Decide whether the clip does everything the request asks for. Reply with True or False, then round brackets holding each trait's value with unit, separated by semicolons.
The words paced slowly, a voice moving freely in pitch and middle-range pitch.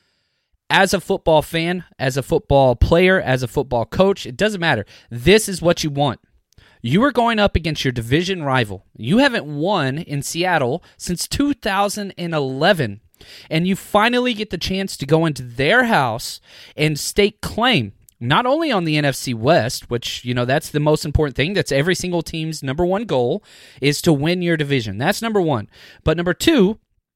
False (180 wpm; 6.1 semitones; 160 Hz)